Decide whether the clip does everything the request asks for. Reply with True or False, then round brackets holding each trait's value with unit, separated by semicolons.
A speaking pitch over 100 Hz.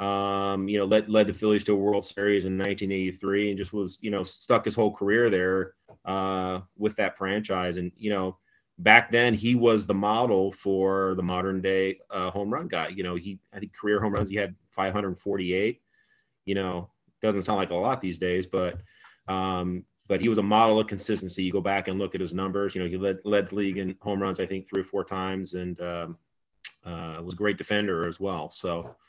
False (95 Hz)